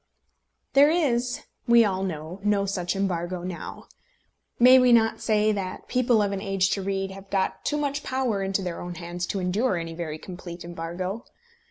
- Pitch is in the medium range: No, high, 195 Hz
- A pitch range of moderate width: Yes, average, 4.6 semitones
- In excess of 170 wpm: Yes, average, 180 wpm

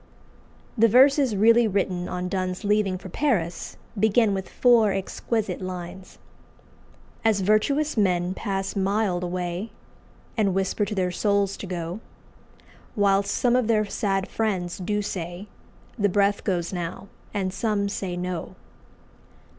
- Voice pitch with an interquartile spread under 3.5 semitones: Yes, average, 2.7 semitones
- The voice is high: Yes, high, 195 Hz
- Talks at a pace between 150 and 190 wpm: No, slow, 135 wpm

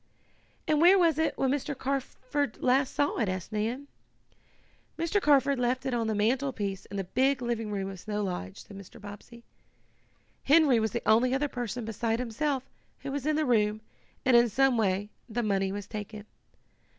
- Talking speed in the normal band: Yes, average, 180 wpm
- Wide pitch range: No, average, 4.6 semitones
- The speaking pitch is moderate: No, high, 240 Hz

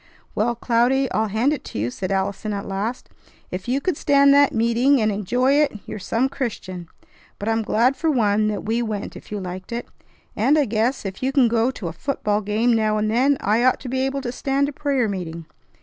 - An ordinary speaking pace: No, fast, 220 wpm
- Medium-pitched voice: No, high, 230 Hz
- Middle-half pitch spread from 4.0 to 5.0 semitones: Yes, average, 4.4 semitones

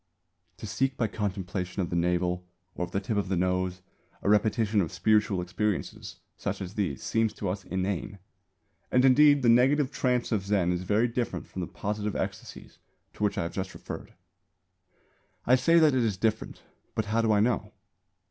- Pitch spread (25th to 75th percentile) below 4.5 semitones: Yes, average, 3.8 semitones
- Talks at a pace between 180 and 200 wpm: Yes, average, 185 wpm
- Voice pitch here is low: Yes, low, 105 Hz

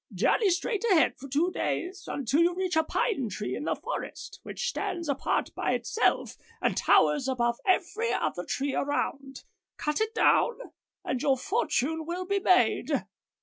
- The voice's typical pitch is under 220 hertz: No, very high, 335 Hz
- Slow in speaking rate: No, average, 160 wpm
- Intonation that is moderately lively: No, wide, 5.9 semitones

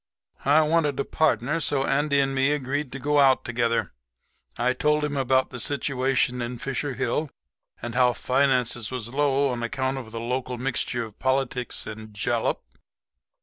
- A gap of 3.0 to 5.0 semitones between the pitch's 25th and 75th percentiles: No, narrow, 2.6 semitones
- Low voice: Yes, low, 130 Hz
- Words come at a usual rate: Yes, average, 165 wpm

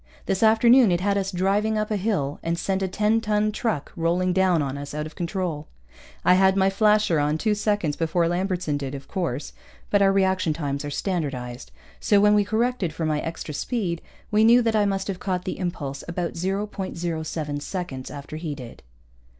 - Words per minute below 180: No, average, 195 wpm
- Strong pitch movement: No, average, 4.8 semitones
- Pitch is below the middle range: No, medium, 185 Hz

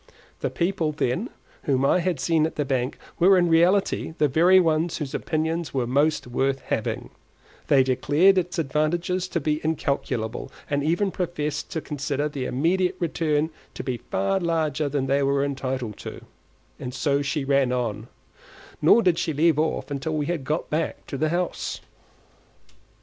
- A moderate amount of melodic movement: Yes, average, 3.6 semitones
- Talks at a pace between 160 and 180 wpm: Yes, average, 165 wpm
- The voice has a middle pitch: Yes, medium, 150 Hz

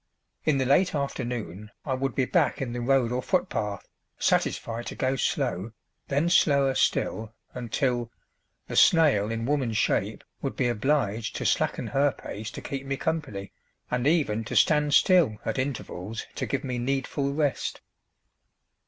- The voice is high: No, low, 130 Hz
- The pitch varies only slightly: No, average, 3.8 semitones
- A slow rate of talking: No, average, 155 wpm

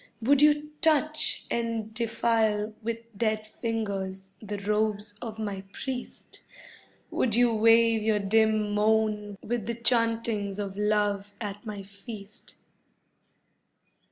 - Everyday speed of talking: No, slow, 115 wpm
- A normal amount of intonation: No, narrow, 1.9 semitones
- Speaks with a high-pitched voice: Yes, high, 220 Hz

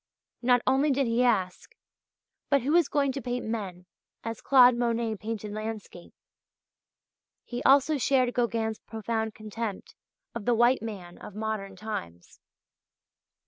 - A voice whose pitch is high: Yes, high, 230 Hz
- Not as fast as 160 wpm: Yes, average, 140 wpm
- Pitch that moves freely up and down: No, average, 2.7 semitones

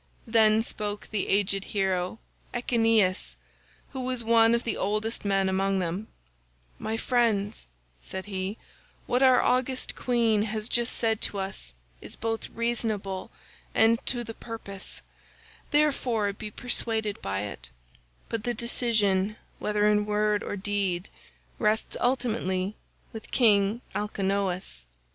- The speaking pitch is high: Yes, high, 215 Hz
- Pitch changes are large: No, average, 2.9 semitones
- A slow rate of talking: Yes, slow, 125 wpm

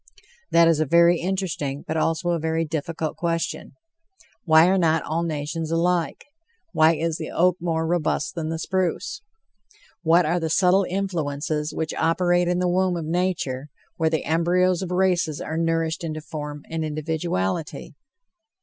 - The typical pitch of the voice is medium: Yes, medium, 165 Hz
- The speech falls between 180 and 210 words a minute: No, average, 160 wpm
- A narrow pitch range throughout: Yes, narrow, 2.0 semitones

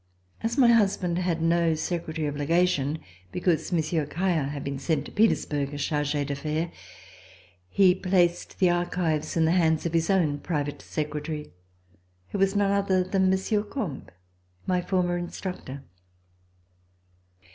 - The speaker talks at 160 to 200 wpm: No, average, 140 wpm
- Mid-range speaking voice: Yes, medium, 170 Hz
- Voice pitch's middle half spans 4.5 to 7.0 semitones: No, average, 3.5 semitones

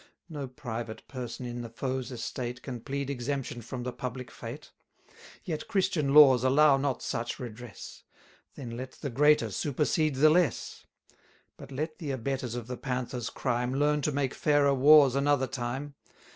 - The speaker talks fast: No, average, 160 wpm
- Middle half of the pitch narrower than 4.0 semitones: Yes, average, 2.9 semitones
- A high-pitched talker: No, low, 130 Hz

